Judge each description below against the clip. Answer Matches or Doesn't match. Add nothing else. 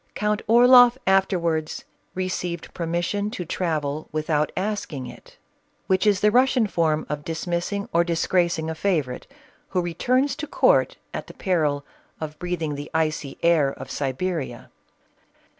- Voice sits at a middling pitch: Matches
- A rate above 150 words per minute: Doesn't match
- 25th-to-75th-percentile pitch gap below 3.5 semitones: Doesn't match